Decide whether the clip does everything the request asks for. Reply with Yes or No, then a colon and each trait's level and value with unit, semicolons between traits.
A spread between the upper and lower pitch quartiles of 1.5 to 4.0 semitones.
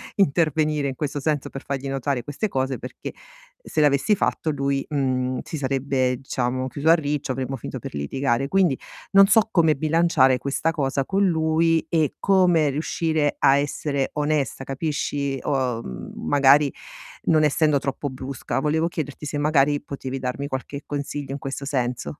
Yes: narrow, 2.6 semitones